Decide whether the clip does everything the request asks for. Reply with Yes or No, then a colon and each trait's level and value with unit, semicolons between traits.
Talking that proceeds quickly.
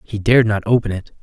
Yes: fast, 245 wpm